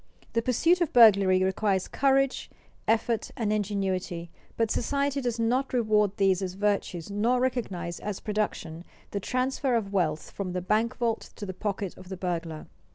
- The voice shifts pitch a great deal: No, average, 4.2 semitones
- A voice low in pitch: No, high, 210 Hz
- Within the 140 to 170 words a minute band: Yes, average, 160 wpm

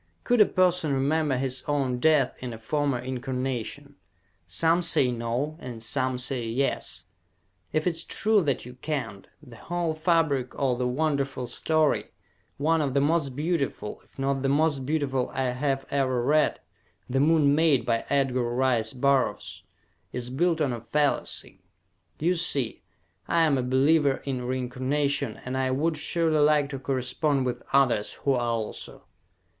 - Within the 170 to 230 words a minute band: No, average, 160 wpm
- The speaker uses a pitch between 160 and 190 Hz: No, low, 135 Hz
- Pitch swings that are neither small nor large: Yes, average, 3.3 semitones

